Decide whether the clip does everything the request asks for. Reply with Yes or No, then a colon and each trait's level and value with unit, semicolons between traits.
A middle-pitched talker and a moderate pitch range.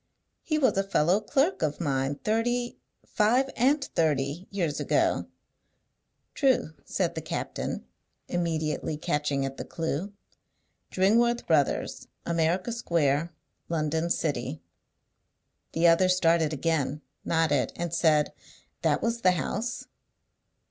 No: medium, 170 Hz; wide, 5.8 semitones